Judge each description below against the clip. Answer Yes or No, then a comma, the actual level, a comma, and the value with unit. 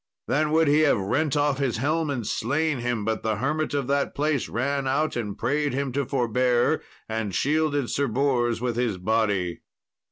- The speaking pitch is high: No, low, 135 Hz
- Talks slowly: No, average, 185 wpm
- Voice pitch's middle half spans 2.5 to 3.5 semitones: No, average, 3.9 semitones